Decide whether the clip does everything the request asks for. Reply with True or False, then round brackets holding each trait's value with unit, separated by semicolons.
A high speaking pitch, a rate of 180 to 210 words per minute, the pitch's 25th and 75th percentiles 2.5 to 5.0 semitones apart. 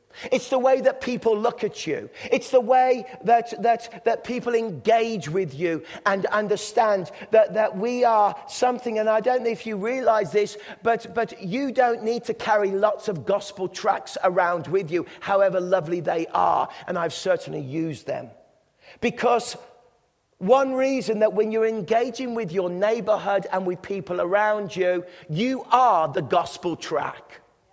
False (215 Hz; 165 wpm; 3.9 semitones)